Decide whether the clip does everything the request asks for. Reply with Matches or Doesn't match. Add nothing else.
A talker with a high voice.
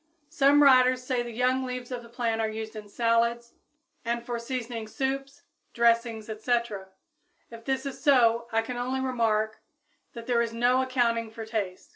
Matches